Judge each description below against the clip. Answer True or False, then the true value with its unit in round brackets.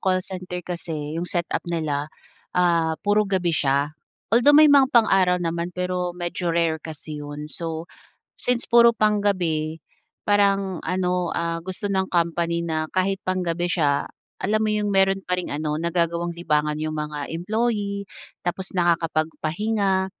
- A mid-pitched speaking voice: True (175 Hz)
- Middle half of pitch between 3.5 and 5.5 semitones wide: False (3.0 semitones)